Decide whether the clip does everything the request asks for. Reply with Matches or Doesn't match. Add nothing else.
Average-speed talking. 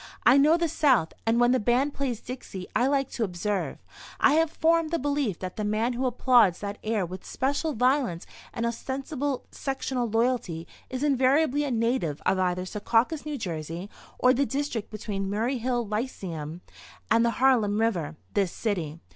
Matches